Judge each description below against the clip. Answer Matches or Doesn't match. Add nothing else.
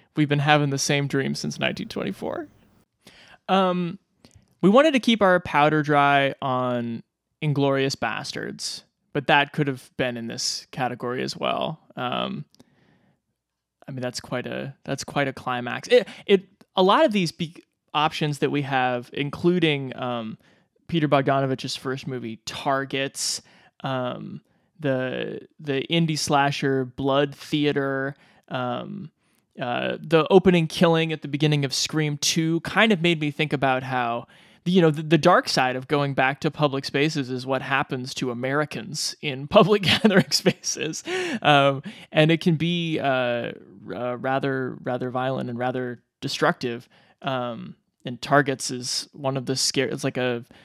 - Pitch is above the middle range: Doesn't match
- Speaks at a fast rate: Doesn't match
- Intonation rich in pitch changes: Doesn't match